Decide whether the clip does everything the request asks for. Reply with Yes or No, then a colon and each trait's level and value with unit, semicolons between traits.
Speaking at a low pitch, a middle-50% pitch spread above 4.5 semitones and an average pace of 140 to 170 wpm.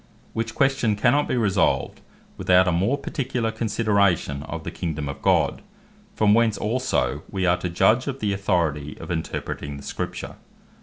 Yes: low, 100 Hz; average, 5.1 semitones; average, 160 wpm